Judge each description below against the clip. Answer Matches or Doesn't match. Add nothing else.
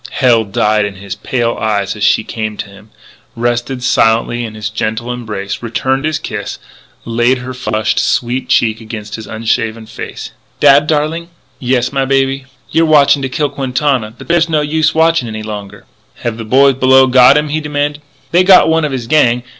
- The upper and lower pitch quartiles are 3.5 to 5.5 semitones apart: Matches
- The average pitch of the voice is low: Matches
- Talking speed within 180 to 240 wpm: Matches